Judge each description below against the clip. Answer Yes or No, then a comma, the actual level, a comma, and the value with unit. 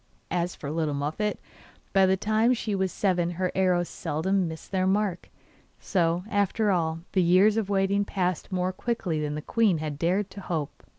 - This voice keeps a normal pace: Yes, average, 180 wpm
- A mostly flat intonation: No, average, 3.2 semitones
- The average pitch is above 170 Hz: Yes, medium, 185 Hz